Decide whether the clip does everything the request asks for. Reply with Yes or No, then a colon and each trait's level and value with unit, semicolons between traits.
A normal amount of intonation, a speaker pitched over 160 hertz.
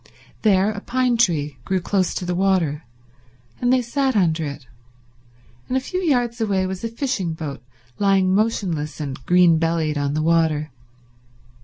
No: wide, 6.1 semitones; medium, 185 Hz